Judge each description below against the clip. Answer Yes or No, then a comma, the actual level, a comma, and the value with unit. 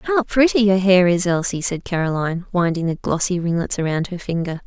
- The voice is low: No, medium, 180 Hz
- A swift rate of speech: No, average, 195 wpm